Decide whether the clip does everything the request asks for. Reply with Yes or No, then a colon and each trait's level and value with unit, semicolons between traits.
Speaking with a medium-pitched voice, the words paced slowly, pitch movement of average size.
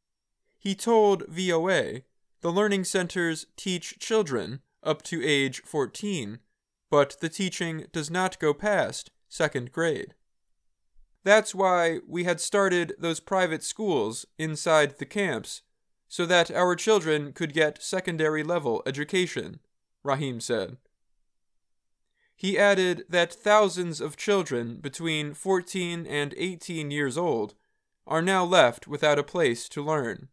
Yes: medium, 170 Hz; slow, 125 wpm; average, 4.2 semitones